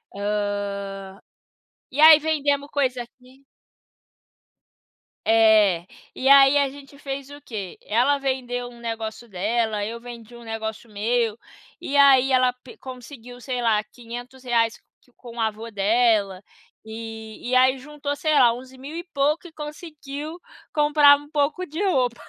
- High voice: Yes, very high, 250 Hz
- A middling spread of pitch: Yes, average, 4.0 semitones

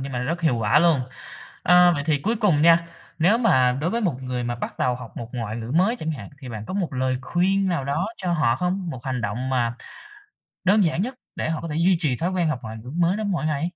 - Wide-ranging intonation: Yes, wide, 6.0 semitones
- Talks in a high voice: No, medium, 155 Hz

